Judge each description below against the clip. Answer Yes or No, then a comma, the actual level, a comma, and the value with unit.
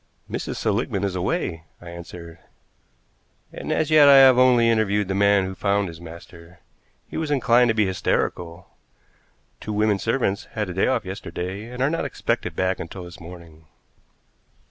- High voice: No, low, 100 Hz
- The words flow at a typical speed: Yes, average, 165 wpm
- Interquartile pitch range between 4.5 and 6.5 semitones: Yes, average, 4.9 semitones